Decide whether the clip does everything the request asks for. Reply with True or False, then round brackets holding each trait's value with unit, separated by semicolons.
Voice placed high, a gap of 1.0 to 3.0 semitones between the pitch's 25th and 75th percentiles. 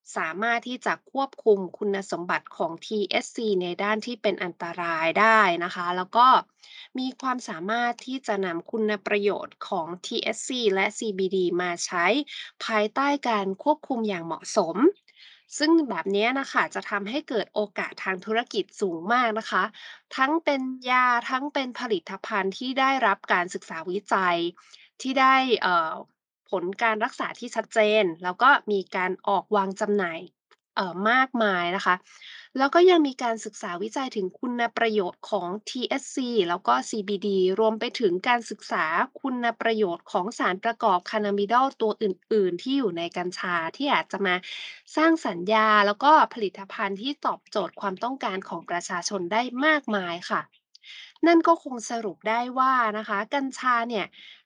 False (220 Hz; 5.0 semitones)